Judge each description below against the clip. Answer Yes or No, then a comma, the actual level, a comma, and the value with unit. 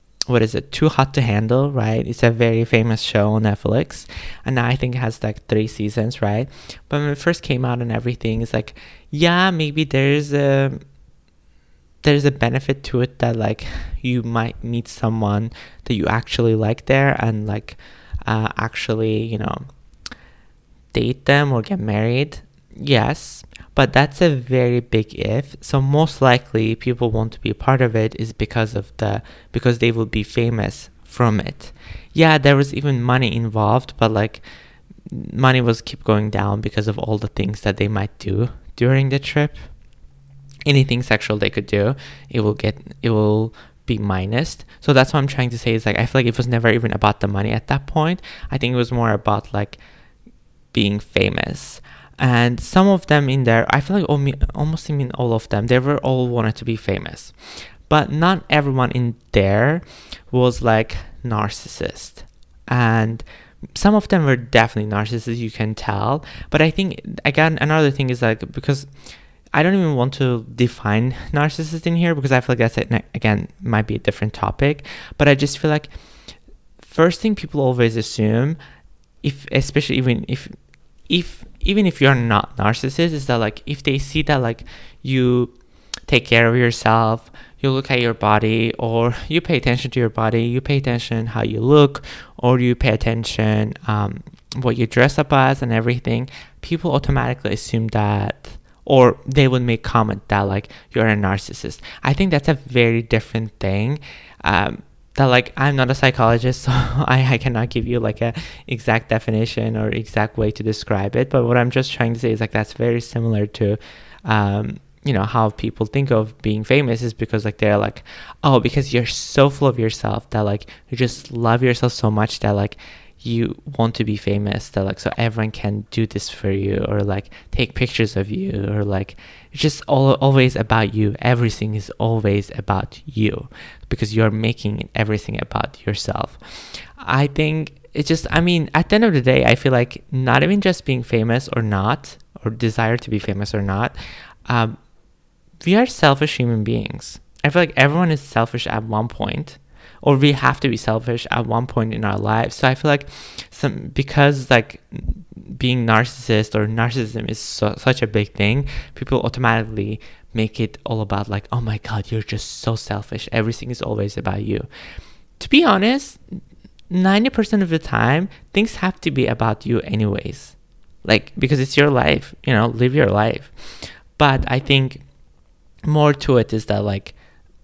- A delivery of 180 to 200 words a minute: Yes, average, 185 wpm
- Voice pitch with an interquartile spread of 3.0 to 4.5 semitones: Yes, average, 4.0 semitones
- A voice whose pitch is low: Yes, low, 120 Hz